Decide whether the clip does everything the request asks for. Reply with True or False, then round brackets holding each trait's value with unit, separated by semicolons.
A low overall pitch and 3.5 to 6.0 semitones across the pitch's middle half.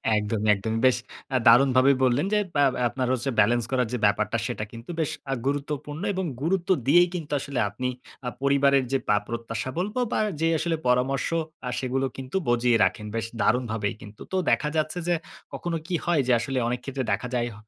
True (130 Hz; 3.9 semitones)